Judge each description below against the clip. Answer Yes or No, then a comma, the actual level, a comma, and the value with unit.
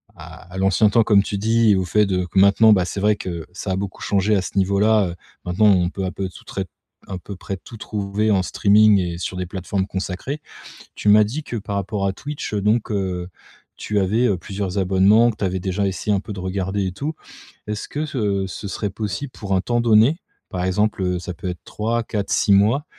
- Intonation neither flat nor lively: No, narrow, 2.3 semitones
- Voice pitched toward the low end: Yes, low, 100 Hz